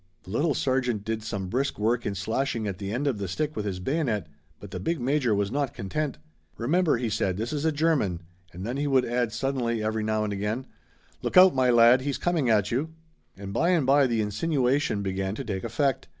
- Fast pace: Yes, fast, 220 wpm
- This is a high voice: No, low, 120 Hz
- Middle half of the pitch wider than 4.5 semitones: Yes, average, 5.1 semitones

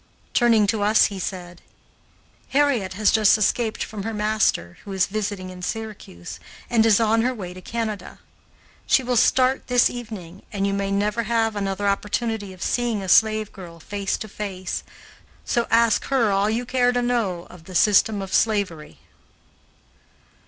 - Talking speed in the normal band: Yes, average, 165 wpm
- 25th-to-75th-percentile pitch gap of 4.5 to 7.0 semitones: No, average, 2.9 semitones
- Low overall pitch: No, high, 210 Hz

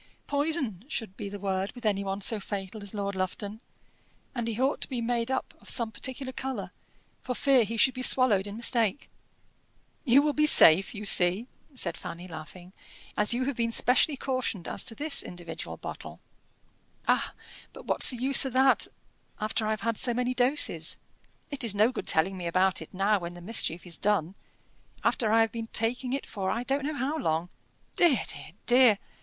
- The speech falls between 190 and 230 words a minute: Yes, average, 195 wpm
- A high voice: Yes, high, 225 Hz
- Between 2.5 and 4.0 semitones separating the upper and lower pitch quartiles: No, average, 4.8 semitones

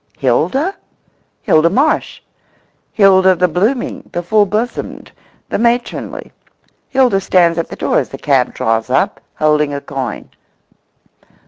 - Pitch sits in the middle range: Yes, medium, 180 Hz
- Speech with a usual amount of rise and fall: No, wide, 6.6 semitones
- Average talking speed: No, slow, 120 wpm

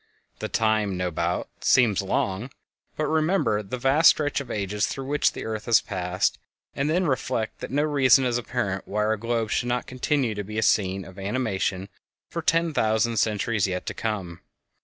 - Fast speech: No, average, 185 wpm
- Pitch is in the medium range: No, low, 110 Hz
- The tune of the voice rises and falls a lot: No, average, 4.9 semitones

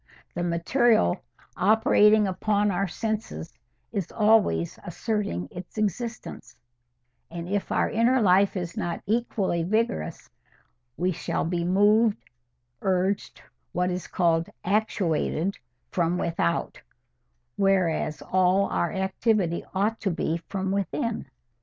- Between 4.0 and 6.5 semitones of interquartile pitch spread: No, average, 3.6 semitones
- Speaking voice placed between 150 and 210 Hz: Yes, high, 190 Hz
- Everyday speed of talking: No, slow, 110 wpm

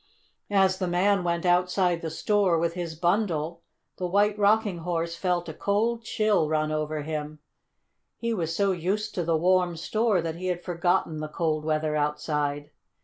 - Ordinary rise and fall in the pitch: Yes, average, 3.4 semitones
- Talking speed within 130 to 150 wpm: No, average, 170 wpm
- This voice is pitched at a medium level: Yes, medium, 175 Hz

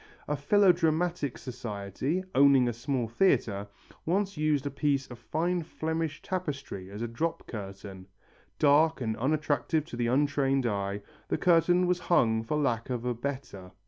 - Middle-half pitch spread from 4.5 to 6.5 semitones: Yes, wide, 5.6 semitones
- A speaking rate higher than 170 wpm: No, average, 150 wpm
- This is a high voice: No, medium, 140 Hz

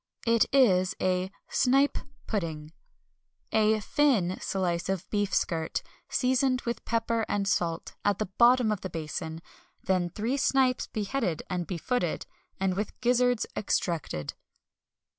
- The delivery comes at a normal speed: No, slow, 125 wpm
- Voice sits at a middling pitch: No, high, 205 Hz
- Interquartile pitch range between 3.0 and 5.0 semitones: No, wide, 5.5 semitones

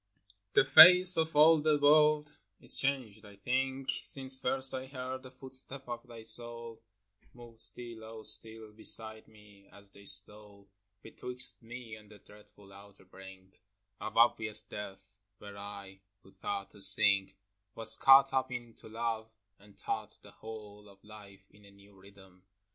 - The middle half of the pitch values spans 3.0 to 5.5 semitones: Yes, average, 4.3 semitones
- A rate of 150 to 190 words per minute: Yes, average, 160 wpm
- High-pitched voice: No, low, 110 Hz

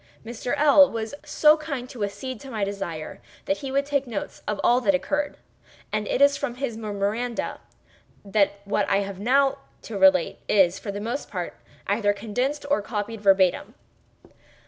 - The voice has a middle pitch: No, high, 220 Hz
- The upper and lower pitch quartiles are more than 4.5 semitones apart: Yes, average, 5.1 semitones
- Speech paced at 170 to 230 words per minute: Yes, average, 175 wpm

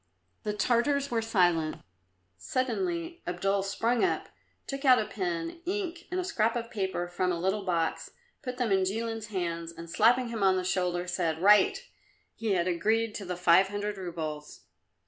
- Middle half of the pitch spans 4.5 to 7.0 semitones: Yes, average, 4.9 semitones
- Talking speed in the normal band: Yes, average, 170 wpm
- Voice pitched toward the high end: Yes, high, 200 Hz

